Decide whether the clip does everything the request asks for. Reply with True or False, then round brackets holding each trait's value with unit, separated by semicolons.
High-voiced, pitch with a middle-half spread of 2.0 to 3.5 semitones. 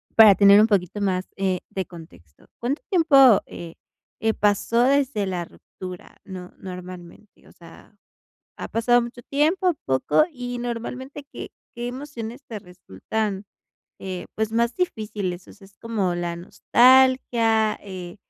False (215 Hz; 4.9 semitones)